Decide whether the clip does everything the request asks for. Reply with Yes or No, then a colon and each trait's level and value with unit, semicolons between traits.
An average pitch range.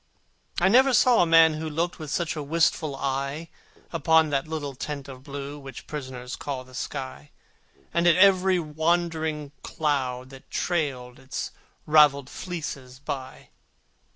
Yes: average, 3.3 semitones